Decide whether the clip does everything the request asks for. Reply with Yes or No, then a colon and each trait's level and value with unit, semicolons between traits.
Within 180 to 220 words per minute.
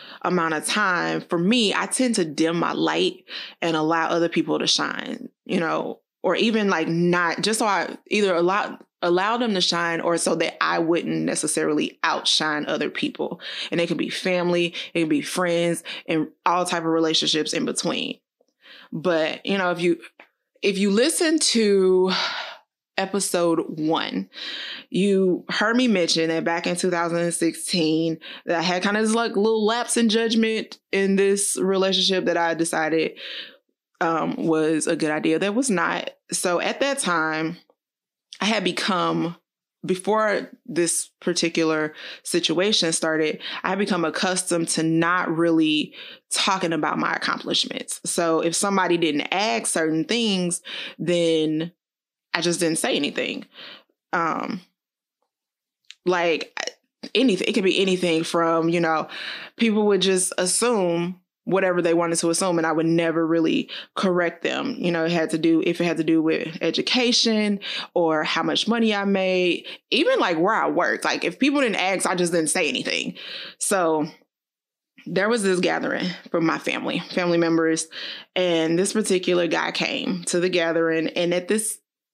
No: average, 160 wpm